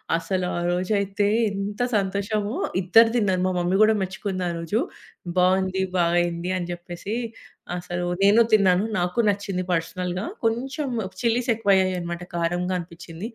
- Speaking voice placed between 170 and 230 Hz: Yes, medium, 185 Hz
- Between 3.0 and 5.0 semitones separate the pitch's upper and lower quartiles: No, narrow, 2.6 semitones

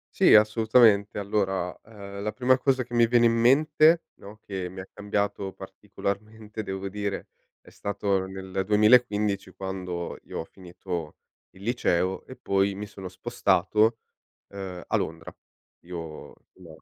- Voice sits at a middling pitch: No, low, 100 Hz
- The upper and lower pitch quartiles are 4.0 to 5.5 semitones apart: No, narrow, 2.6 semitones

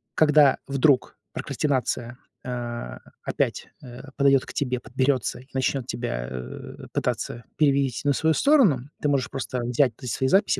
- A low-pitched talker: Yes, low, 130 Hz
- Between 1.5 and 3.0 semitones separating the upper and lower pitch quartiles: Yes, narrow, 2.6 semitones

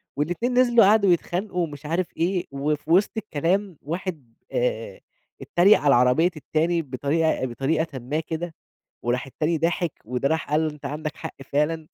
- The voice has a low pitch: No, medium, 160 Hz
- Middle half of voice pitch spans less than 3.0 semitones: No, average, 3.6 semitones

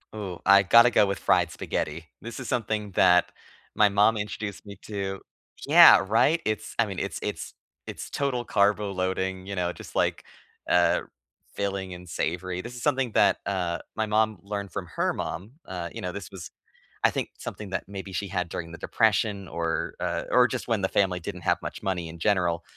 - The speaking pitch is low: Yes, low, 100 Hz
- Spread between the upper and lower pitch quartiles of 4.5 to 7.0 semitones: No, average, 2.9 semitones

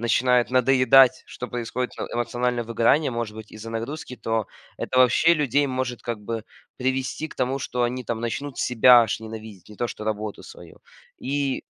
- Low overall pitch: Yes, low, 120 Hz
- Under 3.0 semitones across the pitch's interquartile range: Yes, narrow, 2.4 semitones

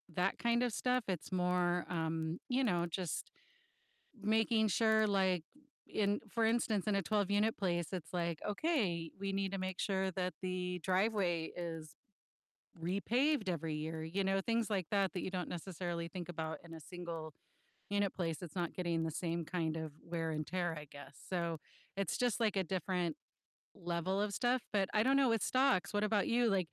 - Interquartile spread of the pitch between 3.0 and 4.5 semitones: Yes, average, 3.6 semitones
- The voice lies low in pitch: No, medium, 185 Hz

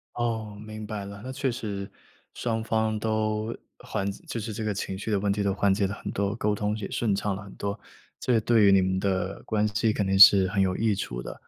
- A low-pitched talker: Yes, low, 105 Hz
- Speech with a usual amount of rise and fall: No, narrow, 1.8 semitones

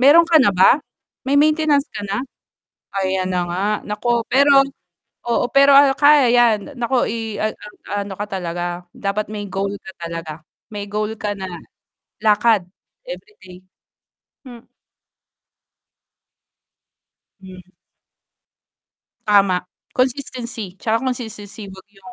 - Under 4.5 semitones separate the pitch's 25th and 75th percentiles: No, average, 5.2 semitones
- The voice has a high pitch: Yes, high, 215 Hz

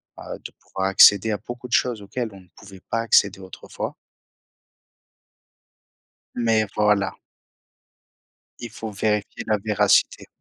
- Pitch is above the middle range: No, low, 105 Hz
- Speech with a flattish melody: Yes, narrow, 2.3 semitones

